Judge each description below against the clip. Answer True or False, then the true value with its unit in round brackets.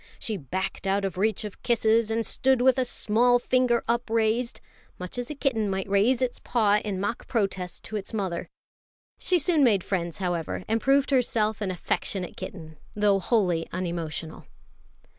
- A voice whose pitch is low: False (215 Hz)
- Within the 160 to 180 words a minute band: True (165 wpm)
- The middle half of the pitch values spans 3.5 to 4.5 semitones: True (4.2 semitones)